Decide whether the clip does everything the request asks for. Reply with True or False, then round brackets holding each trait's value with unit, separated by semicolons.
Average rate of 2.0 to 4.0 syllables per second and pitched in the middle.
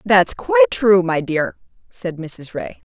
True (3.8 syllables/s; 175 Hz)